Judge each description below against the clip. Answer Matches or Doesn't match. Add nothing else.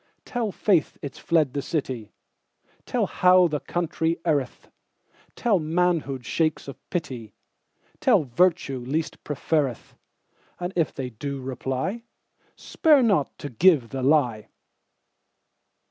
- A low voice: Doesn't match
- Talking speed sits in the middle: Doesn't match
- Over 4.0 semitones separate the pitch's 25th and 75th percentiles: Matches